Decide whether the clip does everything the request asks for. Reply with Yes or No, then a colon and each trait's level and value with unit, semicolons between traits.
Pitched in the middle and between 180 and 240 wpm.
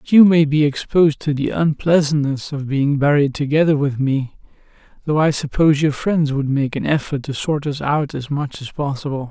Yes: medium, 145 Hz; average, 200 wpm